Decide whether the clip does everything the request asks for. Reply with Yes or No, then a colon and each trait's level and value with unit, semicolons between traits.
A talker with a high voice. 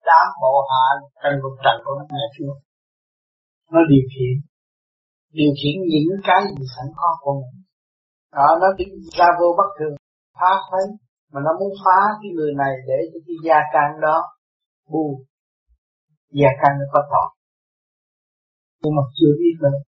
No: medium, 145 Hz